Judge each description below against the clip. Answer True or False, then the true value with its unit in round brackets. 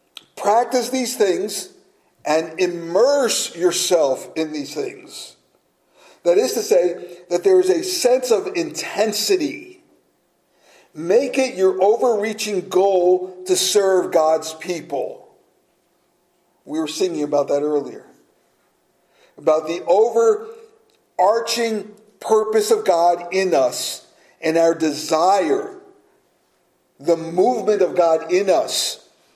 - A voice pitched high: True (200 Hz)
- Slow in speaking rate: True (105 wpm)